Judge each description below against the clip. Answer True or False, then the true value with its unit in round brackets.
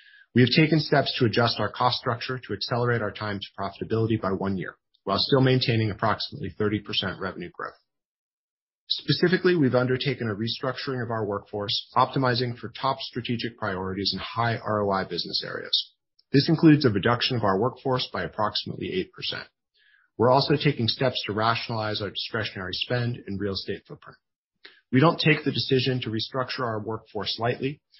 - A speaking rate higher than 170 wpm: False (165 wpm)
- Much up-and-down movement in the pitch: False (3.7 semitones)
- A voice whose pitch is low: True (120 Hz)